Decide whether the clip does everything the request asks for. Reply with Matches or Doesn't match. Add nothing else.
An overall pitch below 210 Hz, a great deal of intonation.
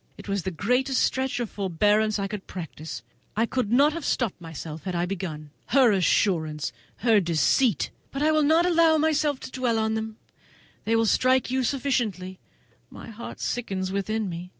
Doesn't match